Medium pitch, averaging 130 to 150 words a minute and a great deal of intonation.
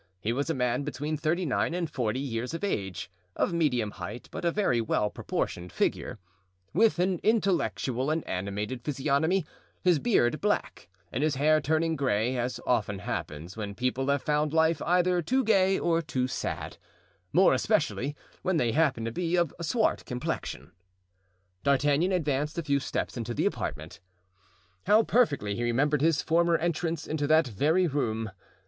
No: medium, 145 Hz; average, 165 wpm; wide, 5.8 semitones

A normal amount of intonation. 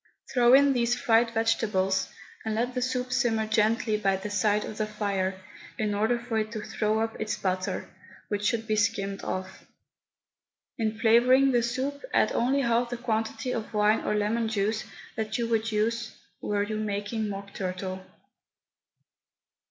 No: narrow, 2.2 semitones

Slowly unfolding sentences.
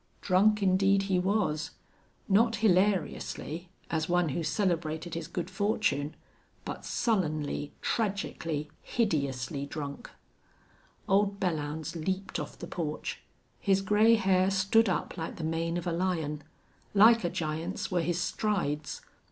Yes: slow, 125 wpm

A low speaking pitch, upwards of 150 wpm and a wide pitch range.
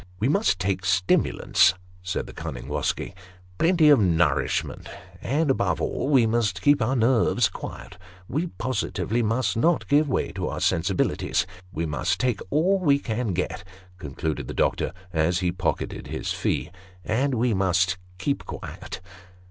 Yes: low, 105 Hz; average, 160 wpm; wide, 6.6 semitones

